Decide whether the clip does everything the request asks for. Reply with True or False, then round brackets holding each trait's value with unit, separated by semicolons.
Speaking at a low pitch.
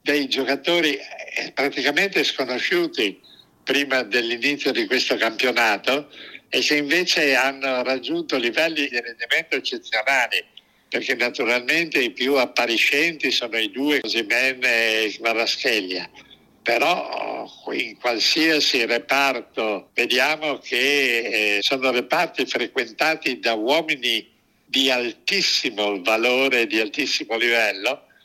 True (130 Hz)